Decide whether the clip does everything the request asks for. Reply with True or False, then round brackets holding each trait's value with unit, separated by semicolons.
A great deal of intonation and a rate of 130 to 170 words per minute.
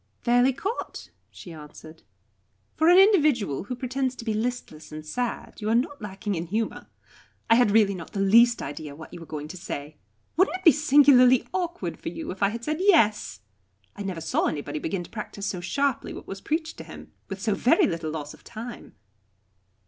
False (7.7 semitones; 200 wpm)